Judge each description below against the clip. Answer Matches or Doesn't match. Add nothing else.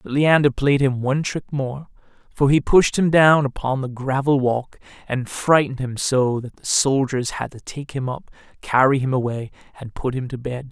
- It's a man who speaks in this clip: Matches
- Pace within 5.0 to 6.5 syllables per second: Doesn't match